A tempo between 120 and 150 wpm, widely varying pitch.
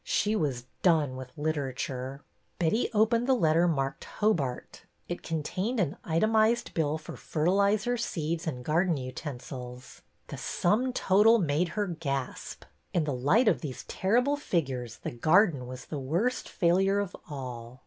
Yes: average, 145 wpm; wide, 7.0 semitones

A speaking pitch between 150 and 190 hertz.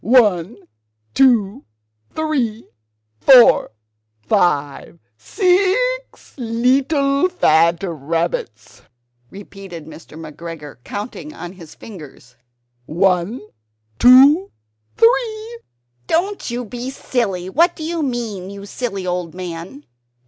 No: high, 215 Hz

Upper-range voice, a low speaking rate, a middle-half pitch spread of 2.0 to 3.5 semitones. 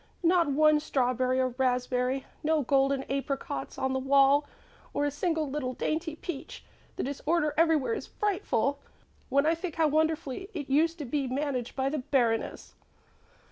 No: very high, 280 Hz; average, 155 wpm; average, 2.9 semitones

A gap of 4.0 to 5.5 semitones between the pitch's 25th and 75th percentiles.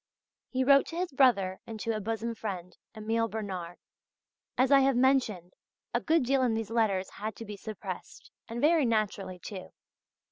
Yes: average, 4.6 semitones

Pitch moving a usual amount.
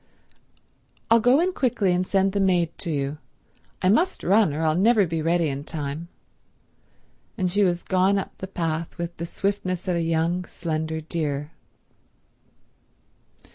Yes: average, 3.4 semitones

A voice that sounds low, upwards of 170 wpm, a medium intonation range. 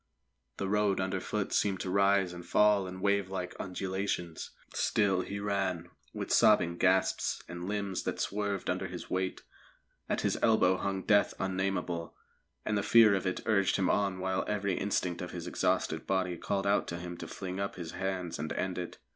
No: very low, 95 Hz; average, 180 wpm; narrow, 1.6 semitones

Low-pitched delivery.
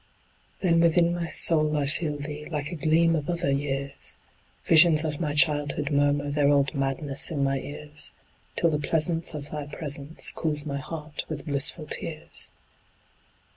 No: medium, 150 Hz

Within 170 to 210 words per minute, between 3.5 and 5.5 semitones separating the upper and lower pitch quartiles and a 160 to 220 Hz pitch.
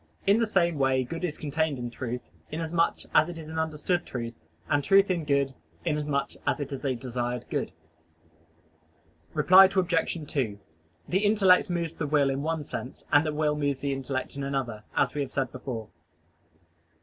No: average, 180 wpm; average, 3.9 semitones; medium, 150 Hz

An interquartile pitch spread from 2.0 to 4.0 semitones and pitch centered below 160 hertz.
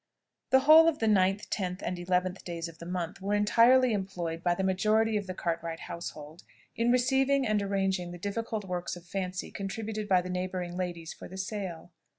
No: average, 3.3 semitones; high, 190 Hz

